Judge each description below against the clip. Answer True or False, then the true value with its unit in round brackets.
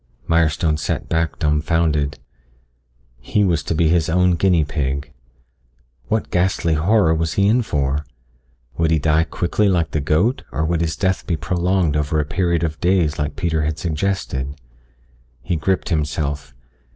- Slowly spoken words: False (155 wpm)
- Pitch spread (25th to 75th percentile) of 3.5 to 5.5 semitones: False (2.9 semitones)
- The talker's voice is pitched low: True (80 Hz)